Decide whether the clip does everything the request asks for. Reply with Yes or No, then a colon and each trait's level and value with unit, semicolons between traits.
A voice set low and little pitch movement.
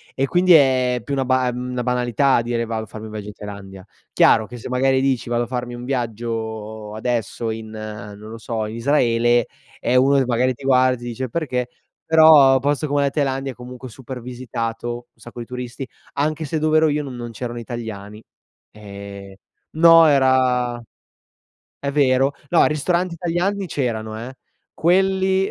No: low, 125 Hz; average, 3.4 semitones